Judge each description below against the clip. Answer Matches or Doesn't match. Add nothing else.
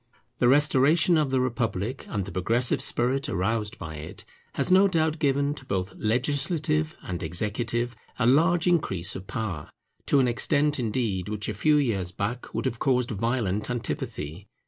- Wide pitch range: Matches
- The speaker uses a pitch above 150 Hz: Doesn't match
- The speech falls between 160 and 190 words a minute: Matches